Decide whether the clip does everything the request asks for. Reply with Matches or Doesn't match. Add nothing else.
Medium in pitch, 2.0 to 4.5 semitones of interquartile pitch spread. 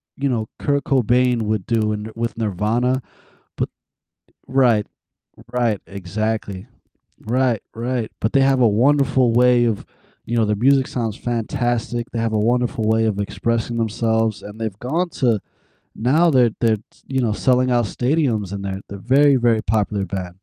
Doesn't match